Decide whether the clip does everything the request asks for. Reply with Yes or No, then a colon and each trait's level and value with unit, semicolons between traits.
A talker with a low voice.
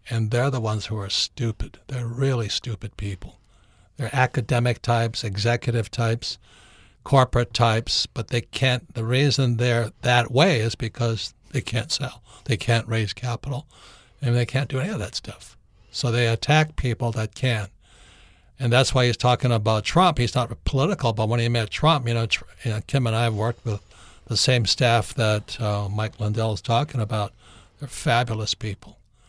Yes: low, 115 Hz